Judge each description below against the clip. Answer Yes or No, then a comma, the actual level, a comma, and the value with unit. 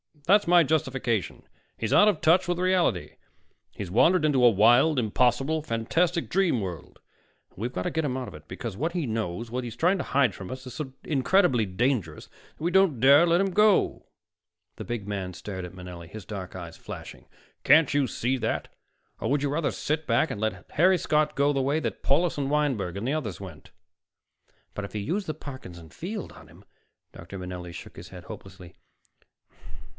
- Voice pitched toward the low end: Yes, low, 130 Hz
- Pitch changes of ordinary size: No, wide, 8.0 semitones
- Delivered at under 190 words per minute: No, average, 200 wpm